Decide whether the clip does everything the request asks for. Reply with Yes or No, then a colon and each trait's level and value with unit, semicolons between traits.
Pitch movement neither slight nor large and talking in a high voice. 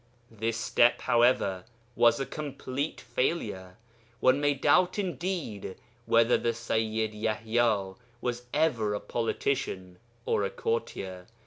No: average, 3.5 semitones; low, 115 Hz